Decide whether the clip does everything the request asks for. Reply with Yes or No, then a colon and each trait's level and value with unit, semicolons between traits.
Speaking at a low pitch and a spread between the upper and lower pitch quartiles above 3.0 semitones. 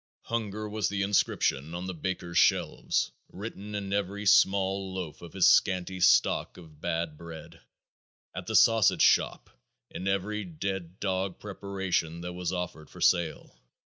No: very low, 95 Hz; narrow, 2.4 semitones